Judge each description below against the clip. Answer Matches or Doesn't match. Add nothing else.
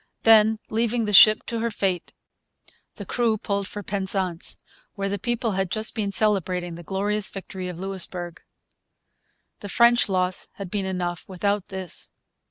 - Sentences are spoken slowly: Doesn't match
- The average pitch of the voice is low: Doesn't match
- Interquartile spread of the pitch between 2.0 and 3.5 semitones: Matches